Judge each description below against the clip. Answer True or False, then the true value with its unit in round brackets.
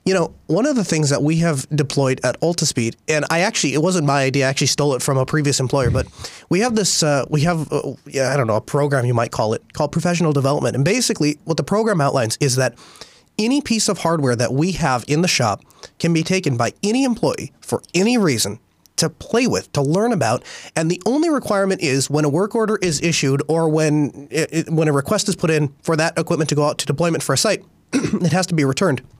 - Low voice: False (155 Hz)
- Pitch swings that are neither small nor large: True (4.1 semitones)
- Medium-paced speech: False (245 wpm)